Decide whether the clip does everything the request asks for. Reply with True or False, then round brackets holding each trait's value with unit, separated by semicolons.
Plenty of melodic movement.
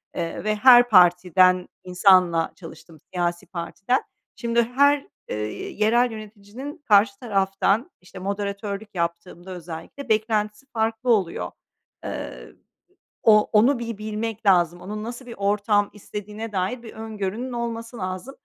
False (3.8 semitones)